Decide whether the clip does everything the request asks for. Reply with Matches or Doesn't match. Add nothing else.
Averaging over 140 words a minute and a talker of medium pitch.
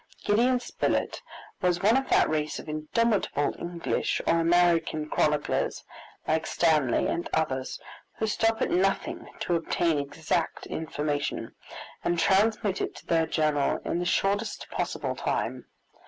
Doesn't match